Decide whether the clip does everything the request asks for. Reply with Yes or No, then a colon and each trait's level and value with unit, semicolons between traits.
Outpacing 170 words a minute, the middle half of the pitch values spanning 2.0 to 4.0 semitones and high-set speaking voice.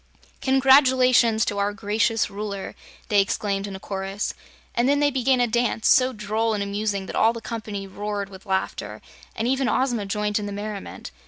Yes: average, 180 wpm; average, 3.3 semitones; high, 215 Hz